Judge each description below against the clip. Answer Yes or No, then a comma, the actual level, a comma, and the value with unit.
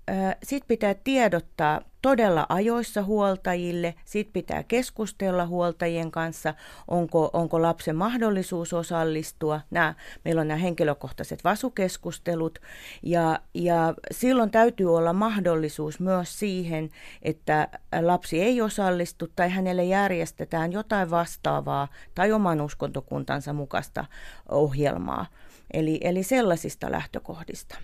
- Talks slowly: No, average, 105 wpm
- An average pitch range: Yes, average, 3.5 semitones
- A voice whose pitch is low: No, medium, 175 Hz